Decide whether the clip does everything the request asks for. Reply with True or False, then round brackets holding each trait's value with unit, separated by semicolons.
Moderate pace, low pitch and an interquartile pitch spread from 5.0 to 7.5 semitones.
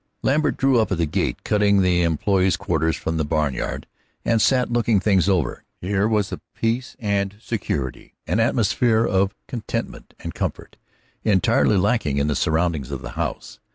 True (165 wpm; 100 Hz; 5.3 semitones)